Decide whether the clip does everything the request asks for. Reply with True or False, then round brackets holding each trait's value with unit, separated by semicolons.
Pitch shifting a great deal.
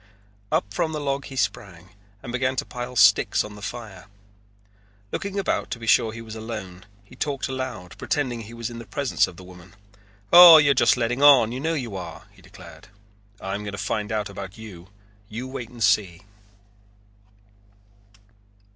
False (4.4 semitones)